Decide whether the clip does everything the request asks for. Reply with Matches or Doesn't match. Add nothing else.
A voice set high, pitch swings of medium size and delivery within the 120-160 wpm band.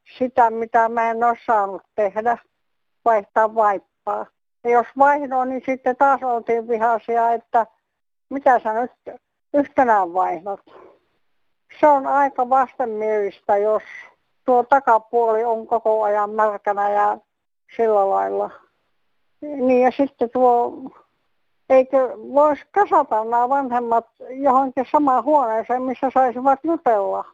Doesn't match